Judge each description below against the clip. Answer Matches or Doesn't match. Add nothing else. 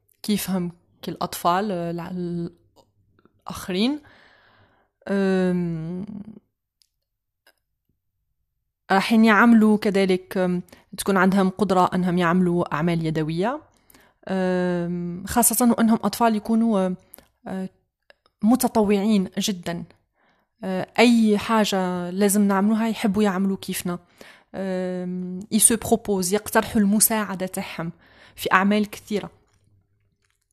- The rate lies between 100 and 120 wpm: Doesn't match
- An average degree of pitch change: Matches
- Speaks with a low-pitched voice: Doesn't match